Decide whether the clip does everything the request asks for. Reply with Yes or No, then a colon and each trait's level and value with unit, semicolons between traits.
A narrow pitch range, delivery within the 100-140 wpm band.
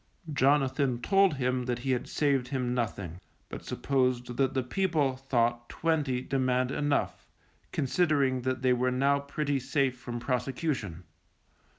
Yes: narrow, 2.2 semitones; slow, 135 wpm